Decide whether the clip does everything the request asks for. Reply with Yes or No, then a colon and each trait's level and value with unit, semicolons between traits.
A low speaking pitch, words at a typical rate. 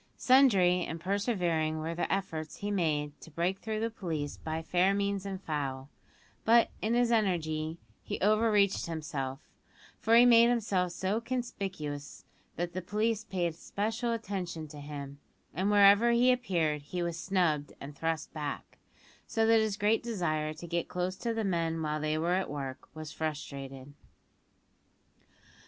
No: medium, 180 Hz; average, 160 wpm